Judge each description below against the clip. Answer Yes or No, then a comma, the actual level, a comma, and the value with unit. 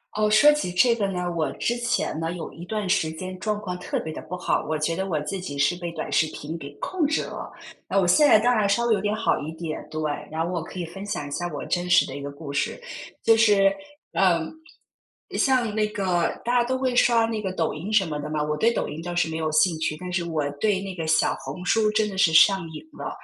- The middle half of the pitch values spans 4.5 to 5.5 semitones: Yes, average, 4.9 semitones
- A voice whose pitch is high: No, medium, 180 Hz